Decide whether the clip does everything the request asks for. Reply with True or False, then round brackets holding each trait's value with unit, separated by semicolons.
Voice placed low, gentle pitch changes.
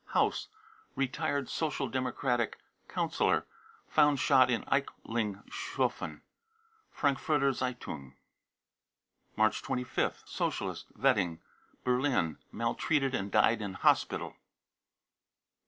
False (130 Hz; 3.9 semitones)